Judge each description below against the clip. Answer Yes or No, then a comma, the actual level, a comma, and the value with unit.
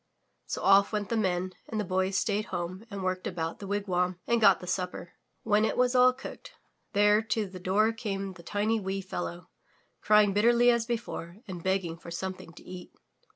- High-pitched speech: Yes, high, 195 Hz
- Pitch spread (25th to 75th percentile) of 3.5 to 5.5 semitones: No, average, 2.9 semitones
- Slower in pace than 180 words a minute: No, average, 195 wpm